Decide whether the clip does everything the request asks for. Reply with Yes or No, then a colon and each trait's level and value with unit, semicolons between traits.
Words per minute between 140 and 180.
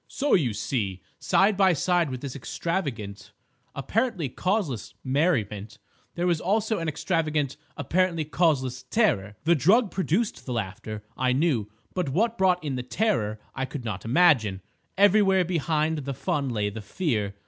Yes: average, 150 wpm